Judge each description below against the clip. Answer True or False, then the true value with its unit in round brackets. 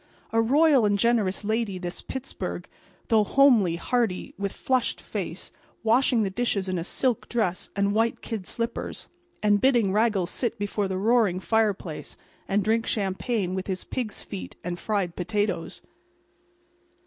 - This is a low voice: False (210 Hz)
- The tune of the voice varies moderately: True (3.6 semitones)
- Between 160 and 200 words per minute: False (145 wpm)